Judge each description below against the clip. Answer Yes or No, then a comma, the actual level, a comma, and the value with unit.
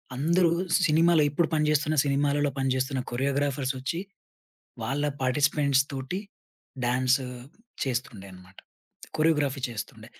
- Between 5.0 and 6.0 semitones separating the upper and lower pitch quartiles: No, narrow, 2.6 semitones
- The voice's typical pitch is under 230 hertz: Yes, medium, 140 Hz